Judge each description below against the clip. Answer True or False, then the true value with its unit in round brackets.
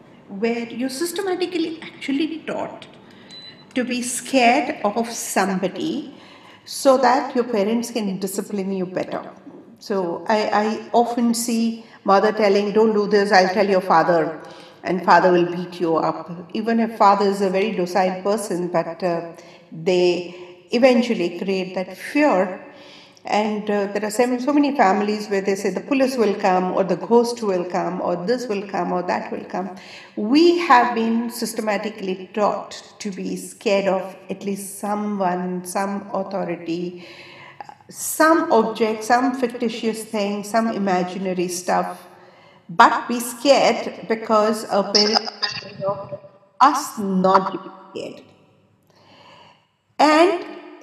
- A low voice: False (205 Hz)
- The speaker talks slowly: True (130 wpm)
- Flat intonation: False (4.1 semitones)